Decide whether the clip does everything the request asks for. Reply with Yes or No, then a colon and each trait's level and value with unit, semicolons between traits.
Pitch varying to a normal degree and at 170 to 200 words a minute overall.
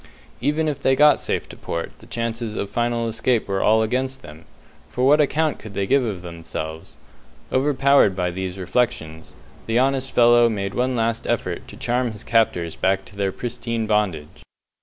Yes: average, 4.8 semitones; average, 180 wpm